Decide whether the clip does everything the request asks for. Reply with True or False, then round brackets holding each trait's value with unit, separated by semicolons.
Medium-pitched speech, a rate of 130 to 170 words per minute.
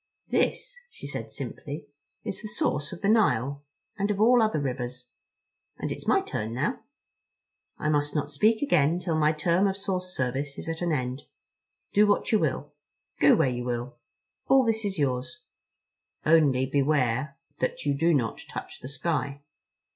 True (145 Hz; 165 wpm)